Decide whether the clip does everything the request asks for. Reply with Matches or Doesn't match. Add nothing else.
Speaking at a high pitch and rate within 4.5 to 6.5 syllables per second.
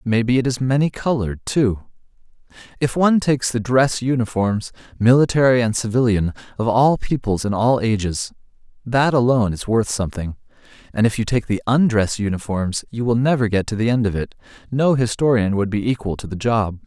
Doesn't match